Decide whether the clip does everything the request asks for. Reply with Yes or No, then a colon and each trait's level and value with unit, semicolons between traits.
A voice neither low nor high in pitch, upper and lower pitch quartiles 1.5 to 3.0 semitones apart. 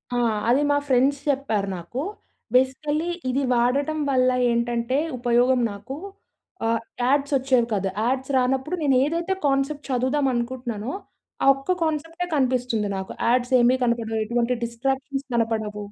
No: very high, 255 Hz; average, 2.7 semitones